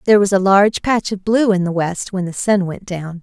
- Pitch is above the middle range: Yes, high, 195 Hz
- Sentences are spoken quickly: Yes, fast, 280 wpm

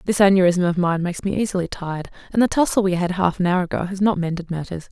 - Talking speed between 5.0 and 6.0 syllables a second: No, 6.8 syllables/s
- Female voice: Yes, female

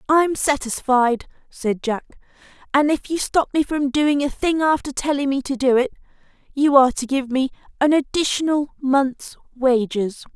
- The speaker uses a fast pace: No, average, 160 wpm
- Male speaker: No, female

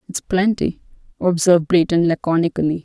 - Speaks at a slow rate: Yes, slow, 105 wpm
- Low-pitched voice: No, medium, 175 Hz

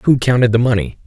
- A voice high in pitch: No, low, 115 Hz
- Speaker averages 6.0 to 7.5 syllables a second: Yes, 6.1 syllables/s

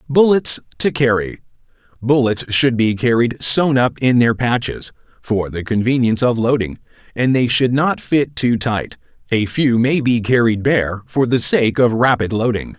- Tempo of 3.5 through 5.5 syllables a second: Yes, 4.5 syllables/s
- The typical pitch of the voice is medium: No, low, 120 Hz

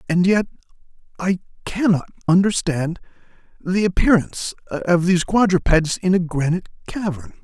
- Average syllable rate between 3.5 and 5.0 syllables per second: No, 5.2 syllables/s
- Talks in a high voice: No, medium, 180 Hz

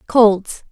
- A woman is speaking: Yes, female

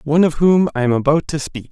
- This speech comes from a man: Yes, male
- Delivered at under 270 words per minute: No, fast, 280 wpm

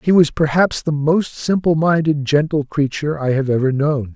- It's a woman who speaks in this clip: No, male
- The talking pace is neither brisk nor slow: Yes, average, 190 wpm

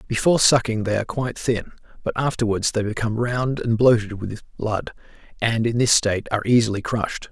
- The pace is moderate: Yes, average, 180 wpm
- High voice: No, low, 115 Hz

